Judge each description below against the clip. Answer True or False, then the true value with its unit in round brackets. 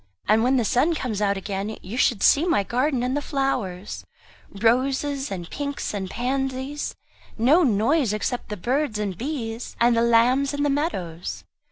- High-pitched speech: True (245 Hz)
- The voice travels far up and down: False (4.8 semitones)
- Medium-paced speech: True (170 wpm)